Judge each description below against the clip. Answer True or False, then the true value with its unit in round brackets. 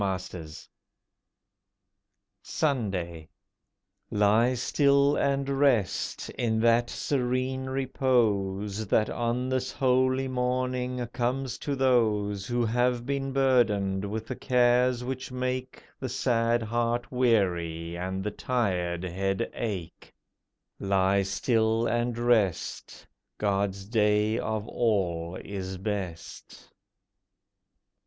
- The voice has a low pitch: True (115 Hz)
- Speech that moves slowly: True (105 wpm)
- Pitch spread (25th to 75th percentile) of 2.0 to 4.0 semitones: False (4.4 semitones)